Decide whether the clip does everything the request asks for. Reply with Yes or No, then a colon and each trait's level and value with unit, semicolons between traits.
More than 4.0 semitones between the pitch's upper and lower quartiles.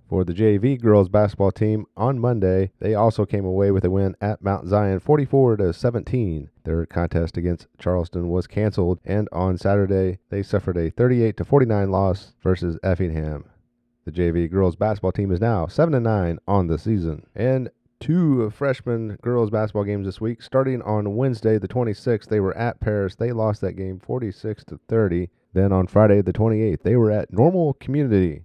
No: average, 3.7 semitones